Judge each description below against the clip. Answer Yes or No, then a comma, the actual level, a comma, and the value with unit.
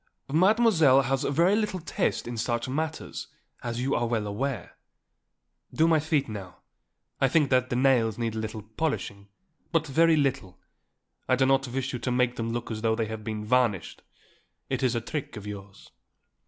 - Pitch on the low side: Yes, low, 125 Hz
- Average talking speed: Yes, average, 180 wpm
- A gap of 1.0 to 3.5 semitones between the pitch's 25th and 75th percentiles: No, average, 4.3 semitones